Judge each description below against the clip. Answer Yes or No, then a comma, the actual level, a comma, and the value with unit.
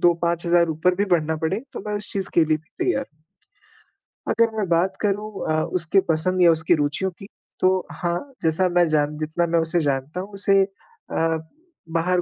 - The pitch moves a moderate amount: Yes, average, 3.1 semitones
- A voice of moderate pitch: Yes, medium, 175 Hz